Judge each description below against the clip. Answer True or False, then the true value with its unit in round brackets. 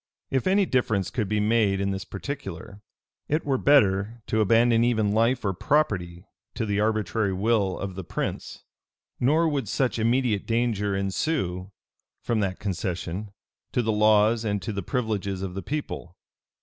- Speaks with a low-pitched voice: True (105 Hz)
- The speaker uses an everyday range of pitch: True (3.6 semitones)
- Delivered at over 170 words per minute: False (160 wpm)